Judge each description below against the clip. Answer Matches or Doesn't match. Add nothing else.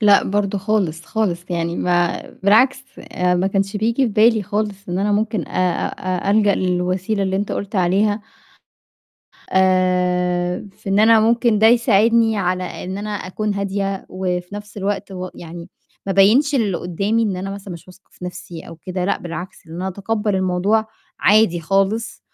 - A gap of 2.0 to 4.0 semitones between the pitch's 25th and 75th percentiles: Matches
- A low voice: Doesn't match